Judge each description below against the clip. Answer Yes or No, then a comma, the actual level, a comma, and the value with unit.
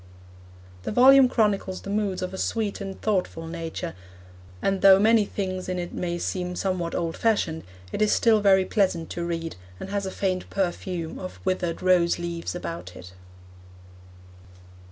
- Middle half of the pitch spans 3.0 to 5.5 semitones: No, narrow, 2.6 semitones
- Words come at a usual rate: Yes, average, 160 wpm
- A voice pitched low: No, medium, 185 Hz